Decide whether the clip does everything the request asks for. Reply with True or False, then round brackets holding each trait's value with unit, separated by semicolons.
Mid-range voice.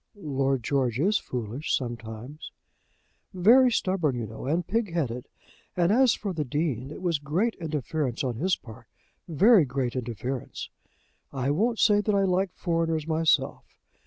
True (155 Hz)